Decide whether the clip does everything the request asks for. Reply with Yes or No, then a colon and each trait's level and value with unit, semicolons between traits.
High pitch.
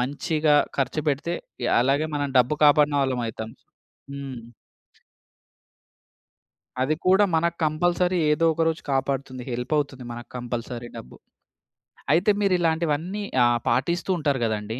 No: medium, 145 Hz